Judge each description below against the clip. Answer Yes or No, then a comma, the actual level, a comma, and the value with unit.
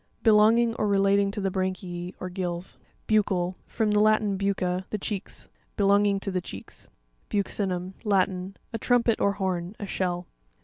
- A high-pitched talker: Yes, high, 195 Hz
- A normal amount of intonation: No, narrow, 2.3 semitones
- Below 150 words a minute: No, average, 160 wpm